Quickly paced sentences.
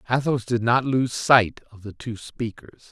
No: average, 185 wpm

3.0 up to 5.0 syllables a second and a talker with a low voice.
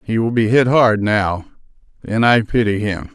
Yes: 4.5 syllables/s; low, 110 Hz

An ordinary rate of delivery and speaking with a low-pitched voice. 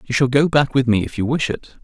No: fast, 325 wpm; low, 130 Hz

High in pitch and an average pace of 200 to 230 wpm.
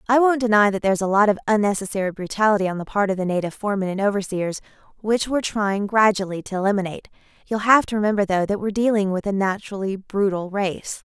Yes: high, 200 Hz; fast, 205 wpm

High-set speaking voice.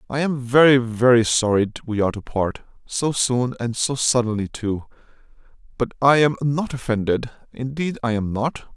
No: low, 125 Hz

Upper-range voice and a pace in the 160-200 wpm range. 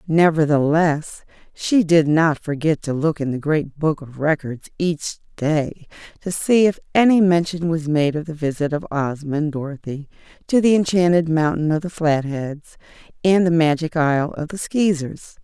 No: medium, 160 Hz; average, 165 wpm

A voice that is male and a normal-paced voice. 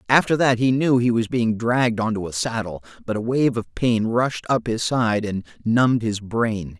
No: male; fast, 210 wpm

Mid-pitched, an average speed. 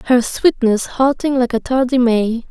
No: high, 245 Hz; average, 170 wpm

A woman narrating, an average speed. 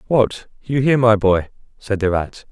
No: male; average, 190 wpm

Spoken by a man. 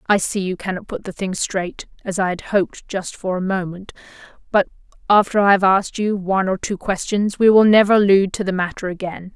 No: female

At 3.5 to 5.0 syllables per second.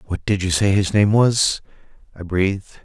Yes: 4.6 syllables/s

